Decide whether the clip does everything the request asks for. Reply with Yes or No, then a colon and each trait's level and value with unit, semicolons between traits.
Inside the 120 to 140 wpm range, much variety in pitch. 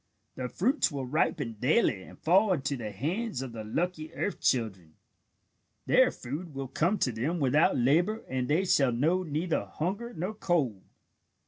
No: average, 160 wpm; wide, 6.2 semitones